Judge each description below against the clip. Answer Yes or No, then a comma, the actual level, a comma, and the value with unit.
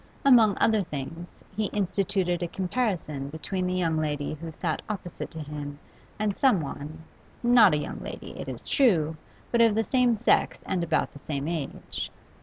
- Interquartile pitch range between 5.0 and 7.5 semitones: Yes, wide, 5.6 semitones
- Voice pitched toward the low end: No, medium, 175 Hz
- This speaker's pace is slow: No, average, 170 wpm